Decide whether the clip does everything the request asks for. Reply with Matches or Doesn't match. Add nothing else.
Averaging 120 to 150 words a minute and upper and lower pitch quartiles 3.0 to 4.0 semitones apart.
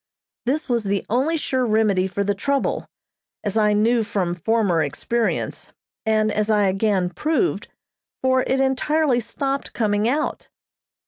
Doesn't match